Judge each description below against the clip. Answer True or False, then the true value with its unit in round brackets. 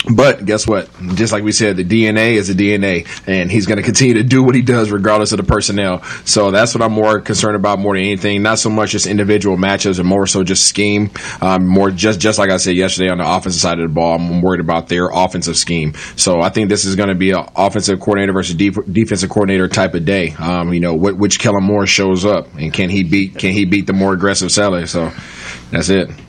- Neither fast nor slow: False (250 wpm)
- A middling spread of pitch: False (2.2 semitones)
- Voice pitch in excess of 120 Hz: False (100 Hz)